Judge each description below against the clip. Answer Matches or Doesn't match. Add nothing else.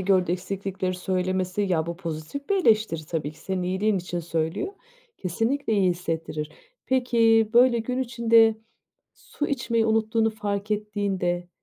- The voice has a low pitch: Doesn't match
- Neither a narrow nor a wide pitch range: Matches